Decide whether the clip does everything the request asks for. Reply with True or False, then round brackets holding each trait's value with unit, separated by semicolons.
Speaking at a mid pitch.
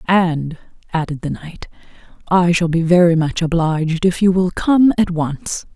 True (170 Hz)